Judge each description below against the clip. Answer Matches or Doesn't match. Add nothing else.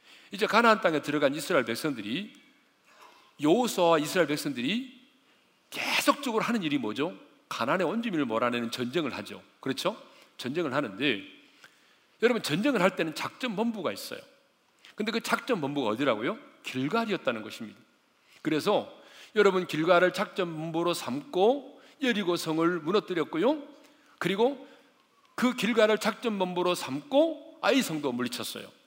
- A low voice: Doesn't match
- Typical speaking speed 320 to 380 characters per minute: Matches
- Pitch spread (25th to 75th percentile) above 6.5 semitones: Matches